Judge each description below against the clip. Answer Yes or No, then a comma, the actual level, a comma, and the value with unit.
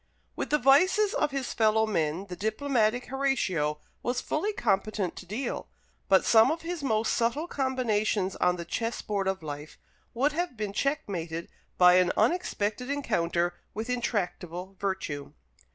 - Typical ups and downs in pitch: No, wide, 6.7 semitones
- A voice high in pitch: Yes, high, 215 Hz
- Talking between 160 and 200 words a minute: No, average, 150 wpm